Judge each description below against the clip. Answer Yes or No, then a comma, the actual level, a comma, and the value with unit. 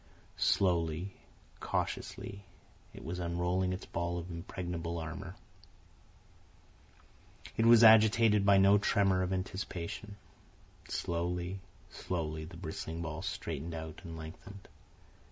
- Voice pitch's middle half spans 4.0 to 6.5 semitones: No, average, 2.8 semitones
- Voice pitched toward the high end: No, very low, 90 Hz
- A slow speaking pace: Yes, slow, 105 wpm